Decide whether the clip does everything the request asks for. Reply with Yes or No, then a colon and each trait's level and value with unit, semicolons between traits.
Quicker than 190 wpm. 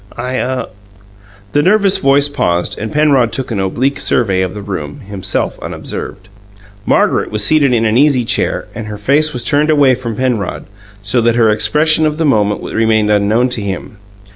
No: average, 185 wpm